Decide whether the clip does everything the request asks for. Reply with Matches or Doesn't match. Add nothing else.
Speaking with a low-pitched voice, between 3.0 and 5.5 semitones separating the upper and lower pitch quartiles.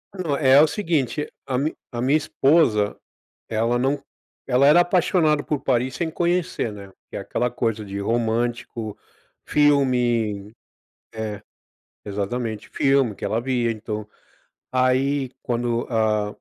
Matches